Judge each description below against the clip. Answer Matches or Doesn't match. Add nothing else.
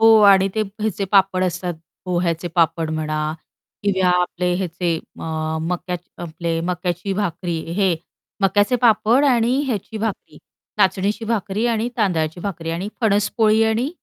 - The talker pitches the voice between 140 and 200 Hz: Matches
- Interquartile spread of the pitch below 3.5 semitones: Doesn't match